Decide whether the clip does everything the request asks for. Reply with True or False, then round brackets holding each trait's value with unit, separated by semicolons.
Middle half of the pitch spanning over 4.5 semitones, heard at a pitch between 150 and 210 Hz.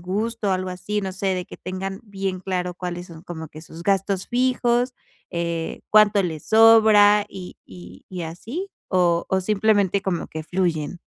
False (3.2 semitones; 190 Hz)